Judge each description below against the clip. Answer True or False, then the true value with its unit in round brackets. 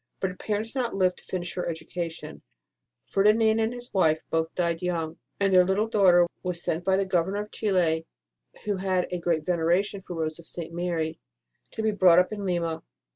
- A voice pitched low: False (180 Hz)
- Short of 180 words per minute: False (200 wpm)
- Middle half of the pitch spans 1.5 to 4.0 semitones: True (3.0 semitones)